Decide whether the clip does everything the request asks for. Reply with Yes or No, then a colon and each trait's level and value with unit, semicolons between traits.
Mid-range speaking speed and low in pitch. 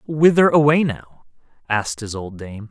Yes: average, 155 wpm; low, 125 Hz